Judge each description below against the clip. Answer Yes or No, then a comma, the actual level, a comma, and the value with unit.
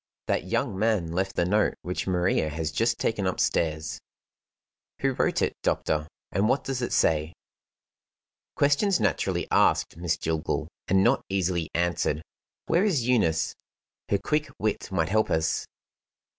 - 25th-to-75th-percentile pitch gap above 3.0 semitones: Yes, wide, 5.6 semitones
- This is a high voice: No, very low, 95 Hz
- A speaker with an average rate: Yes, average, 145 wpm